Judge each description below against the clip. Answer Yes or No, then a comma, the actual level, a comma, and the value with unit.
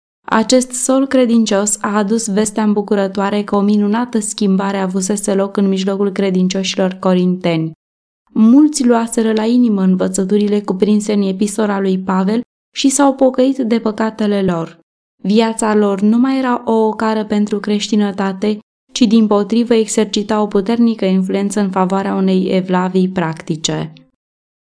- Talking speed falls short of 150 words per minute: Yes, average, 130 wpm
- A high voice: Yes, high, 210 Hz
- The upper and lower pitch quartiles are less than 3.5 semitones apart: Yes, narrow, 2.5 semitones